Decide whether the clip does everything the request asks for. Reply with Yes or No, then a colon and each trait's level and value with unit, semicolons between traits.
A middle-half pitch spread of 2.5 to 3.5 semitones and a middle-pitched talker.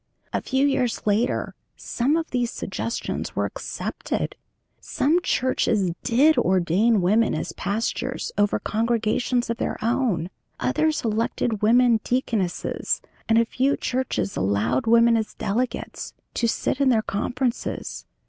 No: average, 3.2 semitones; high, 230 Hz